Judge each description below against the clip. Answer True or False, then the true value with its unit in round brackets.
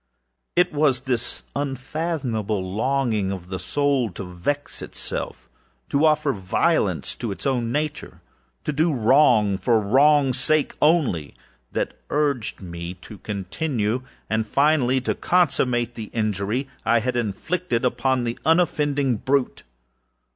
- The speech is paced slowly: True (120 wpm)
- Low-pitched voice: True (125 Hz)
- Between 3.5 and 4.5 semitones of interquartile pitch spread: False (5.3 semitones)